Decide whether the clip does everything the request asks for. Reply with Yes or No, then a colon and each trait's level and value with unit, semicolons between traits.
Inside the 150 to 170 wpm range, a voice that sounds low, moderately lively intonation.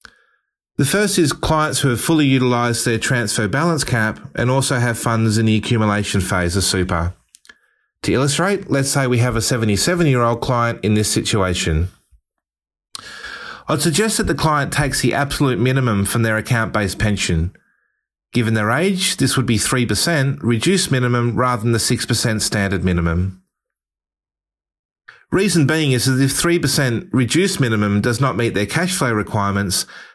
Yes: average, 160 wpm; low, 120 Hz; average, 5.0 semitones